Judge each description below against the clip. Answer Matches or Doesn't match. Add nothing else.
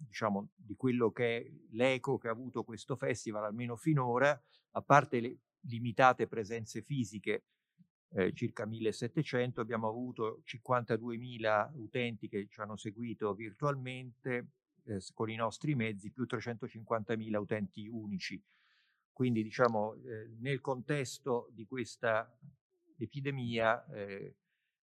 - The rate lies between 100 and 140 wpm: Matches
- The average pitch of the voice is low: Matches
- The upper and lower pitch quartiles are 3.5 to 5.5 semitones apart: Doesn't match